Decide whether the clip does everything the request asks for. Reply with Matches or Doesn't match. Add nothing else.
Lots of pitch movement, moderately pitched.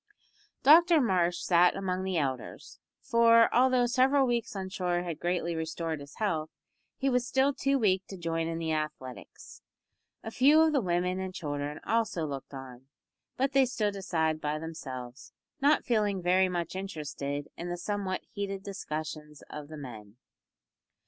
Matches